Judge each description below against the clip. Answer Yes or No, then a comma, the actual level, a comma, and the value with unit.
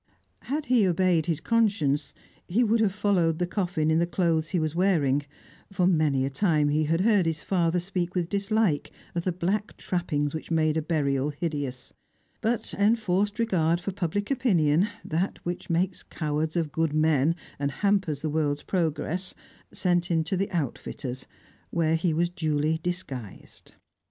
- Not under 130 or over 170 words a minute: Yes, average, 165 wpm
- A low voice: No, medium, 170 Hz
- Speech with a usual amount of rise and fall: Yes, average, 3.7 semitones